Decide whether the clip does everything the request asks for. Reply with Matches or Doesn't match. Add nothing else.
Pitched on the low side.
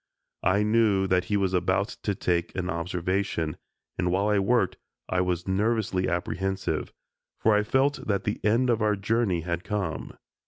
Matches